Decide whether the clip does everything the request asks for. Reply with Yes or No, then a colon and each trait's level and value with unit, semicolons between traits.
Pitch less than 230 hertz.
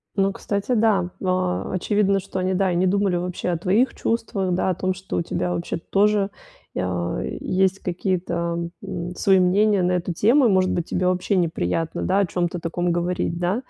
Yes: medium, 185 Hz